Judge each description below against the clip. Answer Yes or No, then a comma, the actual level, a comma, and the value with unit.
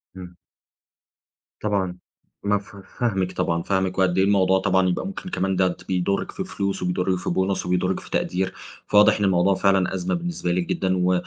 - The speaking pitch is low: Yes, very low, 95 Hz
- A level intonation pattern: Yes, narrow, 1.4 semitones